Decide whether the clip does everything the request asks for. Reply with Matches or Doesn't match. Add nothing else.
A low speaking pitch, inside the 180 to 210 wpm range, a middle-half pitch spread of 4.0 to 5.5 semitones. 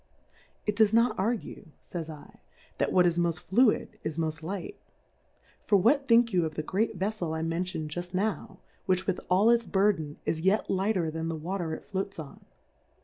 Doesn't match